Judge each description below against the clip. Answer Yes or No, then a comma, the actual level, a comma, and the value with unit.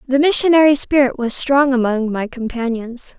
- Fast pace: No, average, 150 wpm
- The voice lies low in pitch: No, very high, 260 Hz